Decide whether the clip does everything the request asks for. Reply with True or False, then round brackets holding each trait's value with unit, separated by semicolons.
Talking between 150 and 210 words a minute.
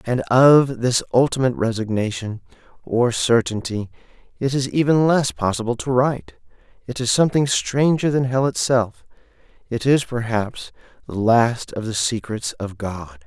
False (140 wpm)